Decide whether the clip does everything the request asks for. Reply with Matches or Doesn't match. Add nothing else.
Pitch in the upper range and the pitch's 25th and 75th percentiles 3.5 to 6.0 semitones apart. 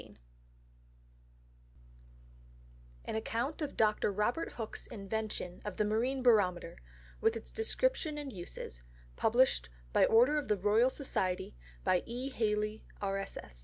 Matches